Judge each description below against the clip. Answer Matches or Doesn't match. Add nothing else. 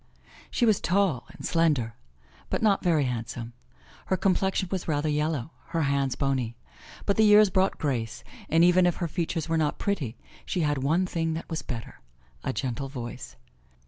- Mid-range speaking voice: Matches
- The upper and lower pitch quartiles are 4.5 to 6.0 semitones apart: Matches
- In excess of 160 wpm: Matches